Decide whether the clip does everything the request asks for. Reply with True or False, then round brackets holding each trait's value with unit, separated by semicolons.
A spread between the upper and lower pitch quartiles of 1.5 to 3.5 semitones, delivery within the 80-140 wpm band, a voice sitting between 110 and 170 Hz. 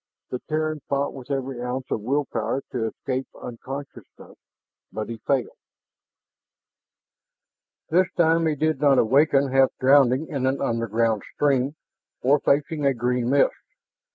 True (2.6 semitones; 135 wpm; 135 Hz)